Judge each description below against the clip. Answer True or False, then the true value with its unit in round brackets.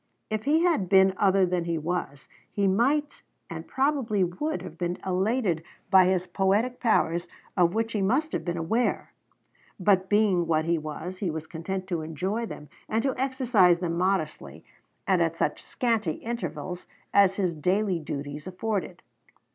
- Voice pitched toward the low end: False (190 Hz)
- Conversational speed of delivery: True (165 wpm)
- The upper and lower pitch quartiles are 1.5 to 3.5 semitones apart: False (4.3 semitones)